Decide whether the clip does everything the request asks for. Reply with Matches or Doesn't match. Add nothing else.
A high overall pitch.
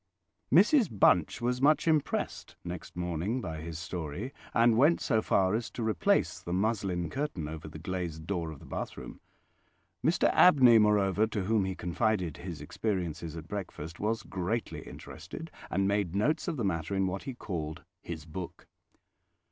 Doesn't match